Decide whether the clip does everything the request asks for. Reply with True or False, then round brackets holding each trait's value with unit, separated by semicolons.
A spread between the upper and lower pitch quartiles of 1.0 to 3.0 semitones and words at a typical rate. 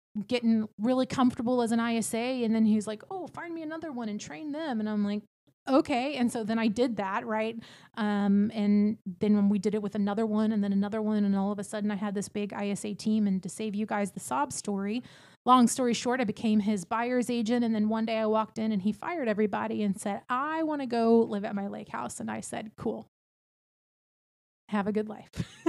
False (2.7 semitones; 235 wpm)